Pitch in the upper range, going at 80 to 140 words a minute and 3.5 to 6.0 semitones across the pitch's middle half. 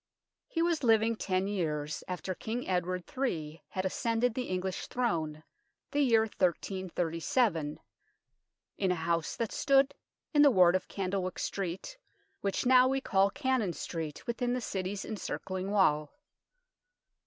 Yes: high, 195 Hz; slow, 135 wpm; wide, 5.4 semitones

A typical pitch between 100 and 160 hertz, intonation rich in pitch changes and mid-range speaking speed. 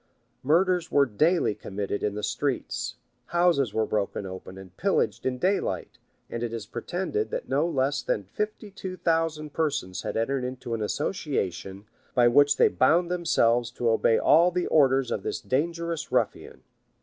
Yes: low, 135 Hz; wide, 7.2 semitones; average, 160 wpm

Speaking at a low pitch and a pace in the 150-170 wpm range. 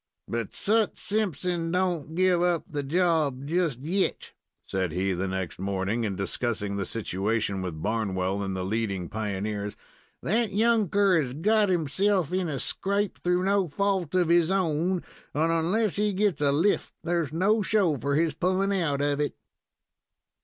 No: medium, 160 Hz; average, 160 wpm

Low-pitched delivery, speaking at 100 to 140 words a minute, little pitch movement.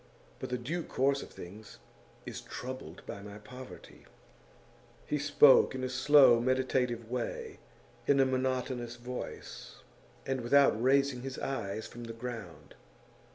Yes: low, 125 Hz; slow, 135 wpm; narrow, 2.3 semitones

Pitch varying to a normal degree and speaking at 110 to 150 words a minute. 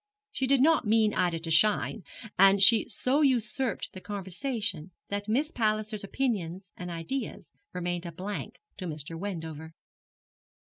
Yes: average, 4.6 semitones; average, 140 wpm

